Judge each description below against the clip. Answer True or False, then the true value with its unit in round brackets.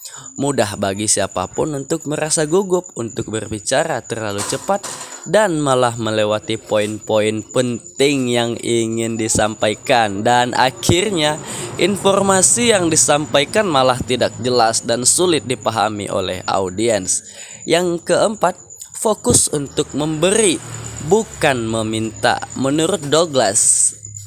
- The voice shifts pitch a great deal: True (6.4 semitones)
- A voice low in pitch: True (125 Hz)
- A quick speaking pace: False (100 wpm)